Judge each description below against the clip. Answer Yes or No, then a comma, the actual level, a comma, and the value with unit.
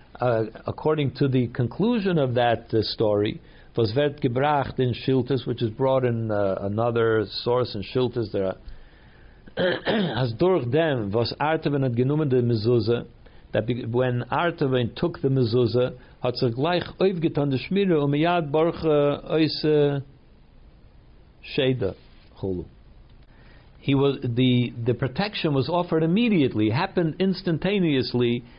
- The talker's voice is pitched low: Yes, low, 130 Hz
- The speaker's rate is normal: No, slow, 120 wpm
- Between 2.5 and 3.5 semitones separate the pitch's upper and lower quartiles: No, average, 4.5 semitones